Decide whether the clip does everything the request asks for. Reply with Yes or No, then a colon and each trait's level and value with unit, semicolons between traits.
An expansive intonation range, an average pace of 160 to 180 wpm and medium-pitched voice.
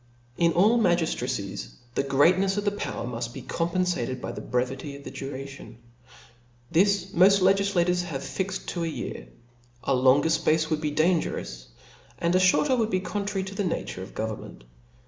Yes: wide, 5.8 semitones; average, 165 wpm; medium, 170 Hz